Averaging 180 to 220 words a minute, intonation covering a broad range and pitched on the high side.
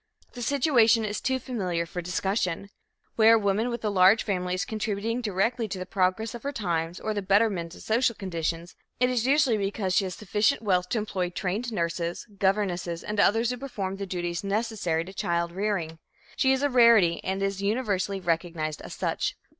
No: average, 190 wpm; average, 4.0 semitones; high, 200 Hz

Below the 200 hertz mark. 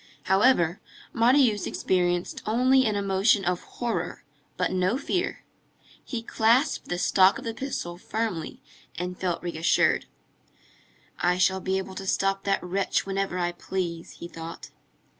Yes: high, 190 Hz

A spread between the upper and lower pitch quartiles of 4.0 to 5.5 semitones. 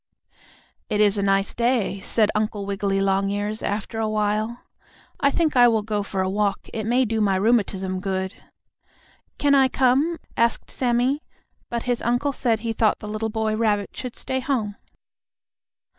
No: average, 3.1 semitones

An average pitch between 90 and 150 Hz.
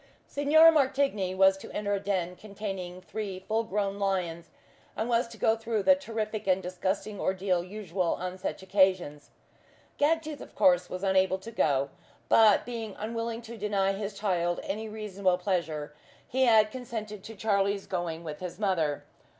No: high, 200 Hz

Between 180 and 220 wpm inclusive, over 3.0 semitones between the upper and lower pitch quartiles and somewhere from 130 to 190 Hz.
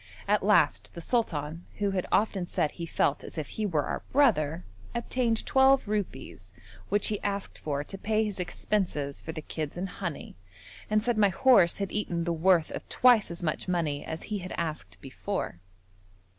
Yes: average, 185 wpm; average, 5.0 semitones; medium, 185 Hz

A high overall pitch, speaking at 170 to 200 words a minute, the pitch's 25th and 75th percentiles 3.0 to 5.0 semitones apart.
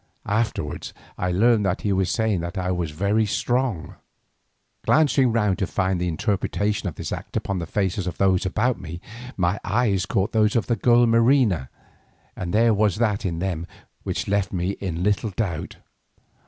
No: low, 100 Hz; average, 175 wpm; average, 3.6 semitones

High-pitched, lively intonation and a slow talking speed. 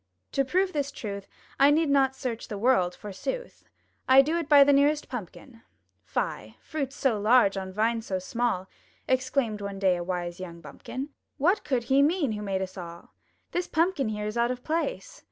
No: high, 245 Hz; wide, 6.0 semitones; average, 190 wpm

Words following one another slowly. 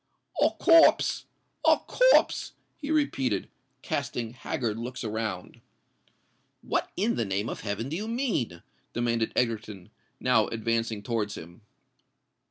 Yes: slow, 120 wpm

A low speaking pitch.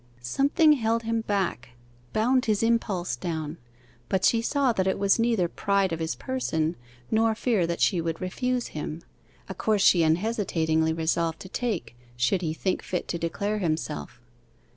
No: high, 190 Hz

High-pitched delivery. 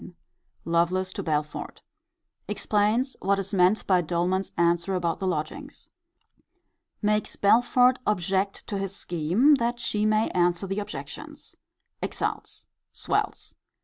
Yes: high, 195 Hz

